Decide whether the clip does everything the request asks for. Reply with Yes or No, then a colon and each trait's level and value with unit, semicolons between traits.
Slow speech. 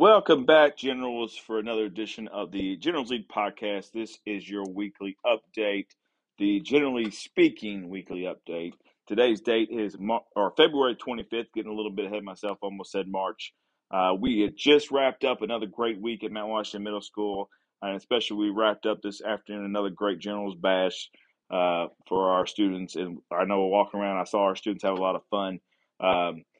No: average, 185 wpm